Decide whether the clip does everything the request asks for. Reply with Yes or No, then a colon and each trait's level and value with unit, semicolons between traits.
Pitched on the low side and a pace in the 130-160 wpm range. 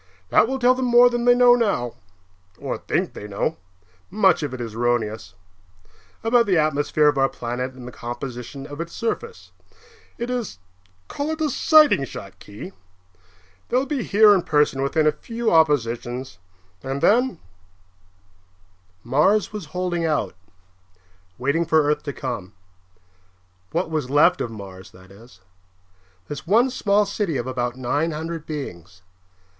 No: medium, 150 Hz; average, 150 wpm